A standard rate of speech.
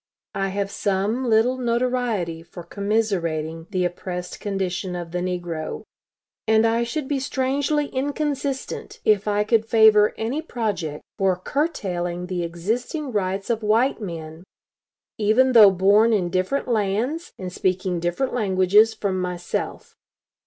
No: slow, 130 wpm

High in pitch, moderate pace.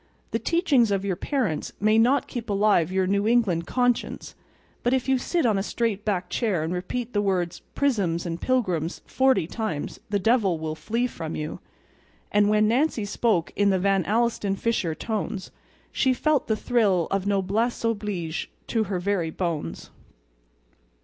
Yes: high, 205 Hz; average, 165 wpm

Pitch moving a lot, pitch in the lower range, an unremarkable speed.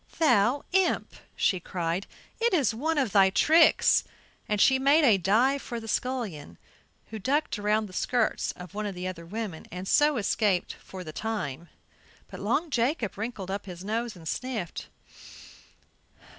No: wide, 6.0 semitones; high, 215 Hz; average, 160 wpm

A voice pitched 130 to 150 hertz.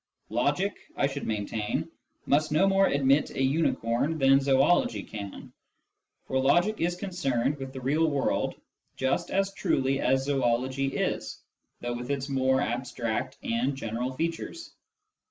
Yes: low, 135 Hz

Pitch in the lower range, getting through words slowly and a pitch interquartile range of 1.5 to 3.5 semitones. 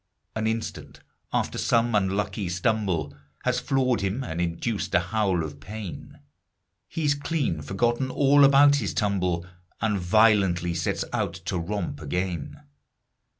No: low, 100 Hz; slow, 130 wpm; average, 5.2 semitones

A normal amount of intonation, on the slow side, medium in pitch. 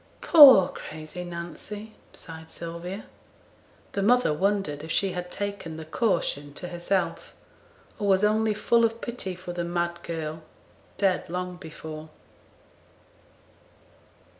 Yes: average, 3.7 semitones; slow, 120 wpm; medium, 180 Hz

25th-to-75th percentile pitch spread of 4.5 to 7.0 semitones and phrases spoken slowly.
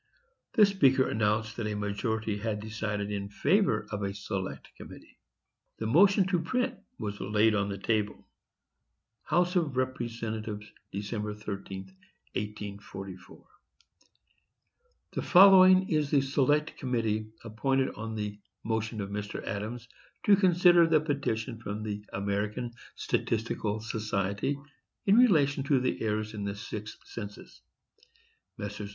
Yes: average, 5.3 semitones; slow, 125 wpm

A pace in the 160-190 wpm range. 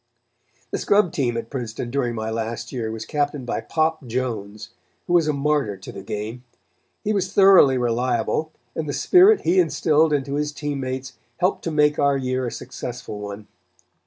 Yes: average, 180 wpm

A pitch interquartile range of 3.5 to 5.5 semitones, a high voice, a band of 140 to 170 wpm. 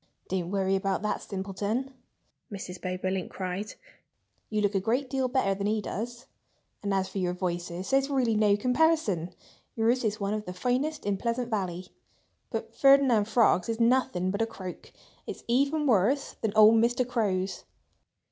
Yes: average, 4.6 semitones; high, 210 Hz; average, 165 wpm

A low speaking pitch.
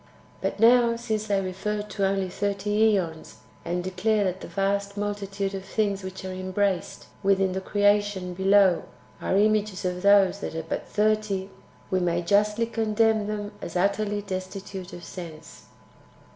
No: high, 200 Hz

